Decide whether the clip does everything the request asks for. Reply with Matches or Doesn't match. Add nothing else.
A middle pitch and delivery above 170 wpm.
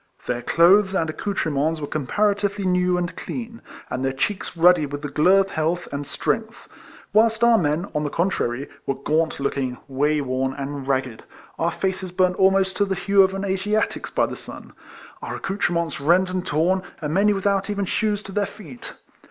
Matches